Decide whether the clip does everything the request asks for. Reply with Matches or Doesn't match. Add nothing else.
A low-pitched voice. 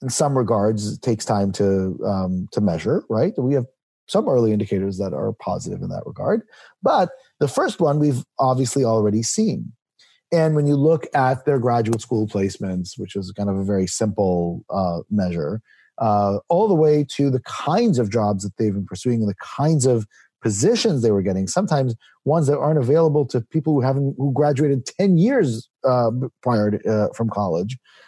Matches